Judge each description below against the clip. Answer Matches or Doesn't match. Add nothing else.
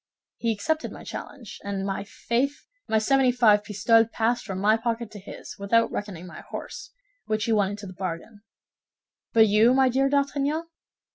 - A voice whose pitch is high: Matches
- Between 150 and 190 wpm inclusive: Matches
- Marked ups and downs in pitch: Doesn't match